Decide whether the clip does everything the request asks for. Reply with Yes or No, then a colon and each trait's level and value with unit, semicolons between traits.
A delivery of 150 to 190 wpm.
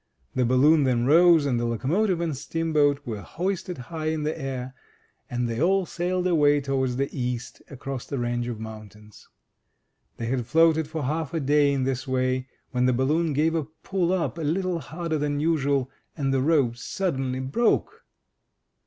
Yes: average, 175 wpm